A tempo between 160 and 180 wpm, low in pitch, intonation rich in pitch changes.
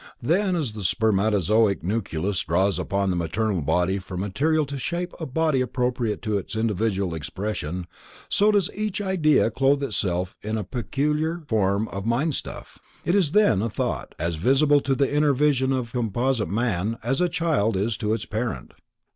Yes: average, 170 wpm; low, 115 Hz; wide, 6.5 semitones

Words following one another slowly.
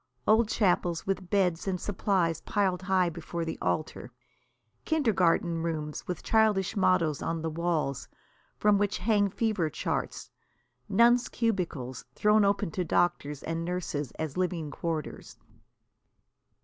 Yes: slow, 125 wpm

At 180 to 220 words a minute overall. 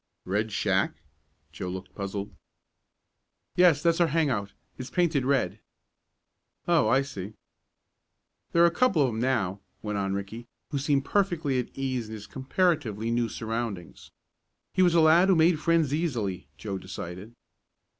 No: average, 155 wpm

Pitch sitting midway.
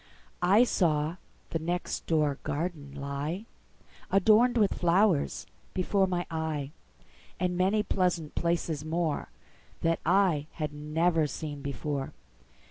Yes: medium, 165 Hz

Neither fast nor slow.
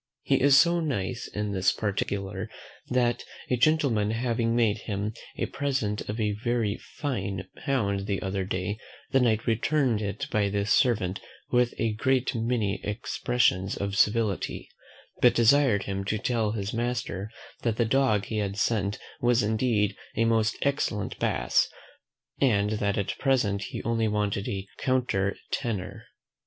Yes: average, 150 wpm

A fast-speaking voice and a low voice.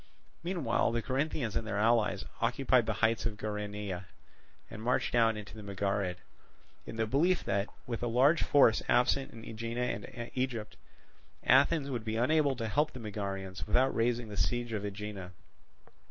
No: average, 165 wpm; low, 115 Hz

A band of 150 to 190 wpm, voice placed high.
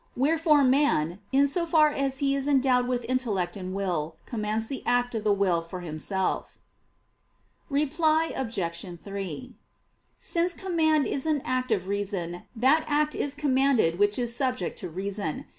Yes: average, 155 wpm; high, 245 Hz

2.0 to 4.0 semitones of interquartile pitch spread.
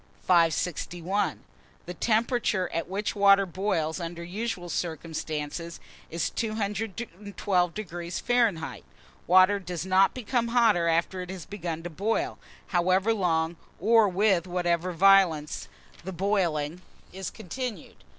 Yes: average, 3.4 semitones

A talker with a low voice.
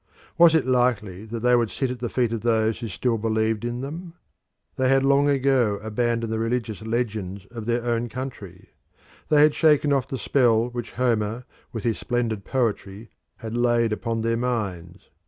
Yes: low, 120 Hz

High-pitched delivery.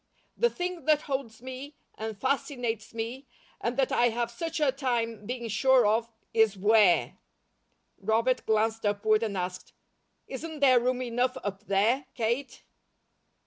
Yes: high, 235 Hz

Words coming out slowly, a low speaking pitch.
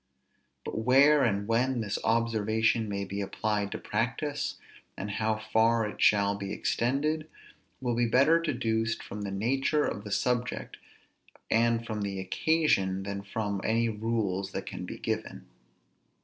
No: average, 150 wpm; low, 110 Hz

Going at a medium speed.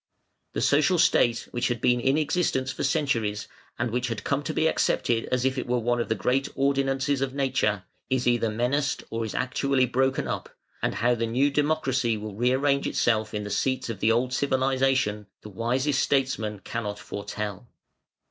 Yes: average, 185 wpm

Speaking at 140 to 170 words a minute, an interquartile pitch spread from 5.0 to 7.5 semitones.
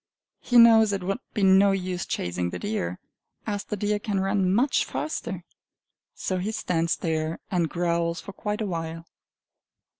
No: average, 160 wpm; average, 3.6 semitones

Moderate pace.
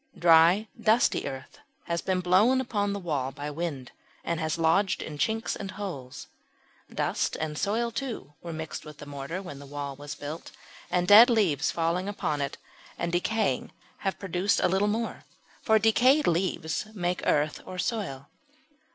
Yes: average, 165 wpm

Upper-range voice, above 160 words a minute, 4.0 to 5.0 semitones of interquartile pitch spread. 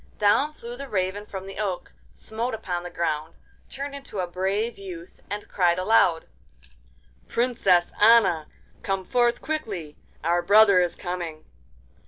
No: high, 195 Hz; average, 140 wpm; average, 4.3 semitones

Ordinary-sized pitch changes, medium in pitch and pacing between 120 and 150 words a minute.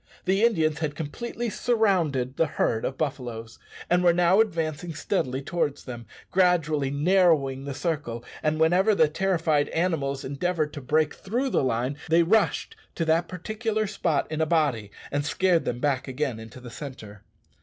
No: average, 4.8 semitones; medium, 155 Hz; average, 165 wpm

